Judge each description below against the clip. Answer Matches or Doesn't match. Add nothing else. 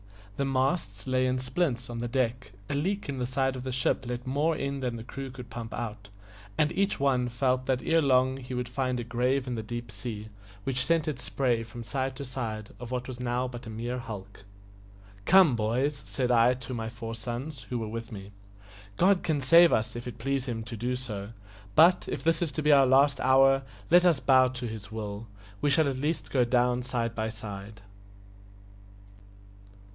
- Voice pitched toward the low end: Matches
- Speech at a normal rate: Doesn't match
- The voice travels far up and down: Doesn't match